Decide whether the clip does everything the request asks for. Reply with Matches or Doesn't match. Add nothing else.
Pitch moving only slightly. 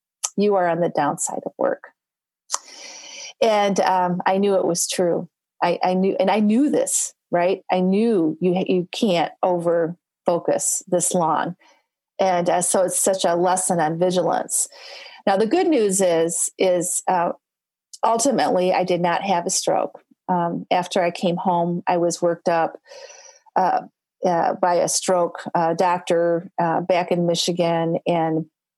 Matches